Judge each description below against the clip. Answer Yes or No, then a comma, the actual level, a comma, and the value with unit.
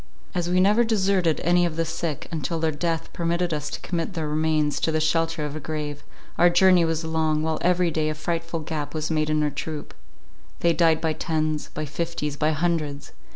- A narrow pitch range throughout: Yes, narrow, 1.8 semitones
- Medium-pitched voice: Yes, medium, 160 Hz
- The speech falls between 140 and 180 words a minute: No, average, 200 wpm